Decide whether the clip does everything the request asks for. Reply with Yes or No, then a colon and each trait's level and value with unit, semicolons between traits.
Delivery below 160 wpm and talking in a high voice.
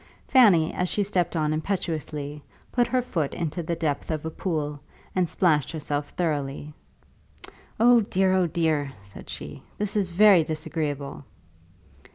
No: average, 145 wpm; medium, 160 Hz